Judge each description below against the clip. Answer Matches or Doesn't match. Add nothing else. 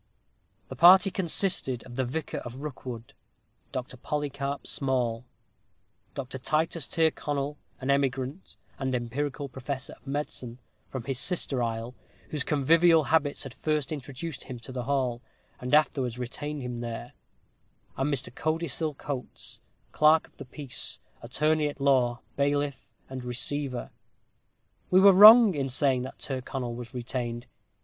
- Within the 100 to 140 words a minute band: Matches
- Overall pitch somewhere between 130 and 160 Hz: Matches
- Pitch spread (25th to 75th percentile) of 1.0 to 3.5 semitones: Matches